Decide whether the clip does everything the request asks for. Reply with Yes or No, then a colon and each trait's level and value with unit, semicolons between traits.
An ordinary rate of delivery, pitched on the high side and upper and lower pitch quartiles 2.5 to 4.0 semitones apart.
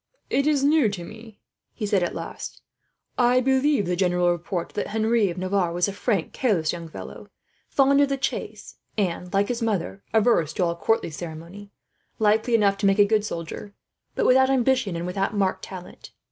No: average, 190 wpm; high, 205 Hz; average, 4.9 semitones